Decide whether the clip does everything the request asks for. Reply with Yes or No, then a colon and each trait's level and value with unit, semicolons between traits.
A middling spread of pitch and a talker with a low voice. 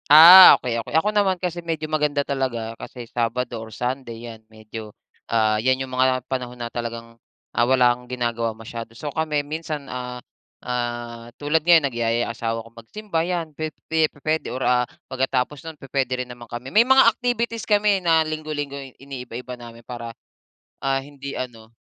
Yes: average, 4.8 semitones; low, 130 Hz